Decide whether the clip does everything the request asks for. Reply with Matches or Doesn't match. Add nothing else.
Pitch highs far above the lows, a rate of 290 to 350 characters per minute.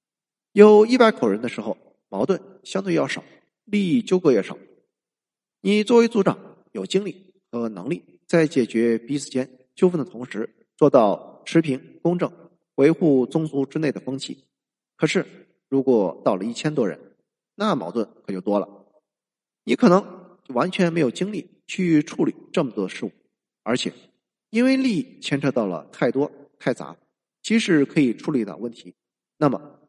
Doesn't match